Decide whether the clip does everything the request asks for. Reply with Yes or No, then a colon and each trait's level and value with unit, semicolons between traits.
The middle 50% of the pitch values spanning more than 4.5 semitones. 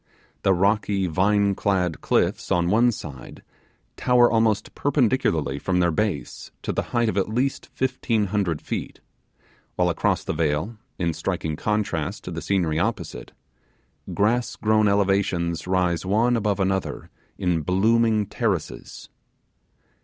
No: average, 4.0 semitones